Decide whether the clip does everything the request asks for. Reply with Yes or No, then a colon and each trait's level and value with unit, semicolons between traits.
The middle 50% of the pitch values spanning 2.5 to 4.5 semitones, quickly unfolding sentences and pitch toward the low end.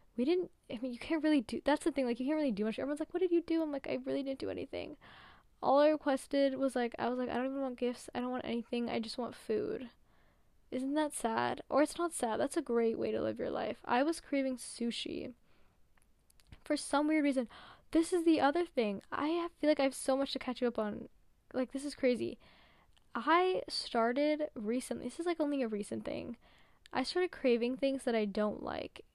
No: average, 4.1 semitones; fast, 235 wpm; very high, 265 Hz